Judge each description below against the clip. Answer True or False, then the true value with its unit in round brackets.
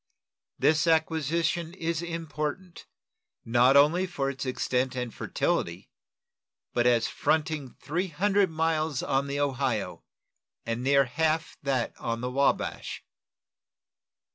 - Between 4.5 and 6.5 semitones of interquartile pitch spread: False (3.9 semitones)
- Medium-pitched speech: True (150 Hz)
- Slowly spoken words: True (115 wpm)